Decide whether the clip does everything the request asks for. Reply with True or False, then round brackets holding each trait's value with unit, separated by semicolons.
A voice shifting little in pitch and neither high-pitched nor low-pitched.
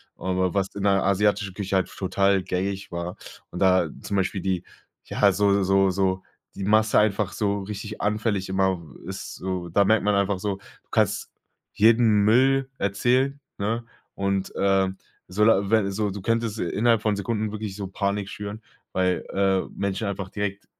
False (1.8 semitones; 100 Hz)